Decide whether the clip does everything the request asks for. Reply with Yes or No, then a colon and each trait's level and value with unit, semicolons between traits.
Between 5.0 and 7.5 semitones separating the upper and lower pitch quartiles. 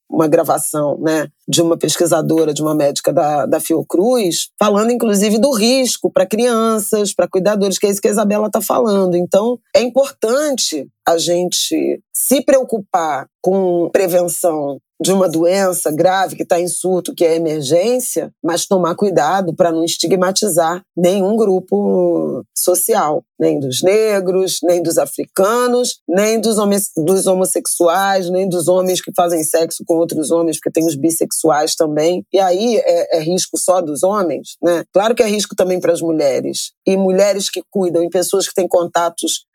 No: average, 3.6 semitones